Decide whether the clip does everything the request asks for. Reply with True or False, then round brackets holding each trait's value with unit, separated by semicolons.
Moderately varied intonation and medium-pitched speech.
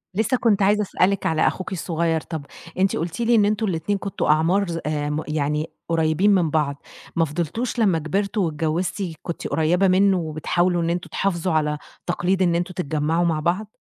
True (3.7 semitones; 175 Hz)